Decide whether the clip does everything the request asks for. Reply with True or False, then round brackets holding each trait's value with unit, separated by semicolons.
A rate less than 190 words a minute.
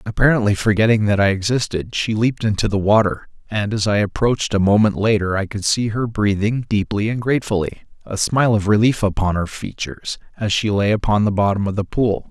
False (200 wpm)